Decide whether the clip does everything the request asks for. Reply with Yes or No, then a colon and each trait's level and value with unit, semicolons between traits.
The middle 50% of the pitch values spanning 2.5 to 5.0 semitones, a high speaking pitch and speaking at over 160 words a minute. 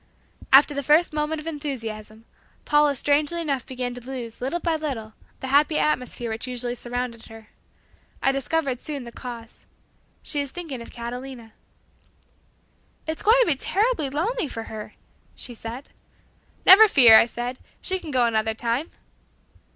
No: average, 4.3 semitones; very high, 265 Hz; average, 155 wpm